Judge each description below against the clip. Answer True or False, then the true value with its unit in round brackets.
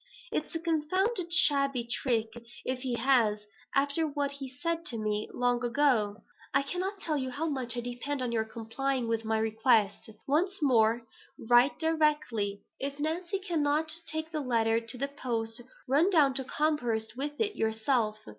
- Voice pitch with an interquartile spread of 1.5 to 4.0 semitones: False (4.8 semitones)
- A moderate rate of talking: True (165 wpm)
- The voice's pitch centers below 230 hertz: False (265 Hz)